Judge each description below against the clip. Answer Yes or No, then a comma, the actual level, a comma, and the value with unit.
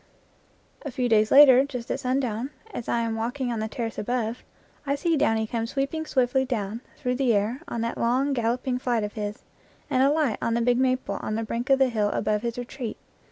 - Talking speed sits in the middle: No, fast, 210 wpm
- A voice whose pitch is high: Yes, high, 245 Hz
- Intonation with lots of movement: No, average, 2.7 semitones